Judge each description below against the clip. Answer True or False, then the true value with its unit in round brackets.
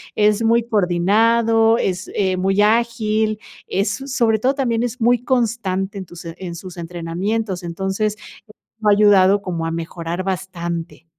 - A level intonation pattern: False (4.0 semitones)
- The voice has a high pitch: True (200 Hz)